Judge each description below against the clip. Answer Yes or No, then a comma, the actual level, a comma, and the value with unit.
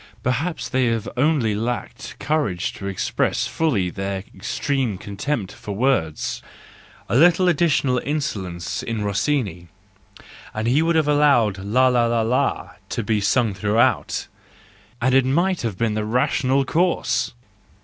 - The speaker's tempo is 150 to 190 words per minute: No, slow, 135 wpm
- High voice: No, low, 120 Hz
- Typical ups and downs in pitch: No, wide, 5.7 semitones